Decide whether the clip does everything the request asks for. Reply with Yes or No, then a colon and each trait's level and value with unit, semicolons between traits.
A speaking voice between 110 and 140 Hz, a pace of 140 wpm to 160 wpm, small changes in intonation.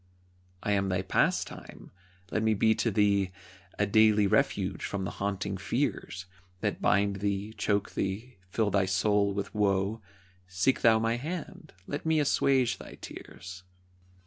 No: low, 100 Hz; average, 145 wpm; narrow, 2.2 semitones